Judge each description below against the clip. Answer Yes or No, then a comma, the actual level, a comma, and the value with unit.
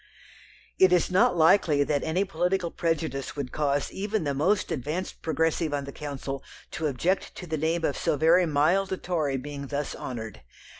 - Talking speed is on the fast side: No, average, 180 wpm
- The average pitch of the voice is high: No, medium, 160 Hz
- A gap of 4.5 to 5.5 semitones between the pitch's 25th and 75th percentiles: No, average, 3.8 semitones